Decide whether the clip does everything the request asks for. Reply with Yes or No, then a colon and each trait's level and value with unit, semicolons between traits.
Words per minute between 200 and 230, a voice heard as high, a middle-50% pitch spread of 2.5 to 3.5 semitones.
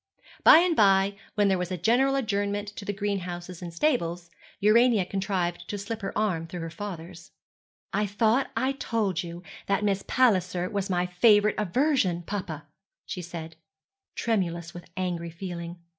No: average, 160 wpm; high, 195 Hz; average, 3.2 semitones